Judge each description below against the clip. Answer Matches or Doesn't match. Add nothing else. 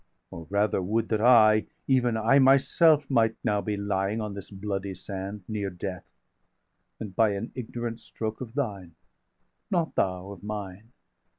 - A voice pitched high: Doesn't match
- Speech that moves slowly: Doesn't match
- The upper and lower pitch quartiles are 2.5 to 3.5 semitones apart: Matches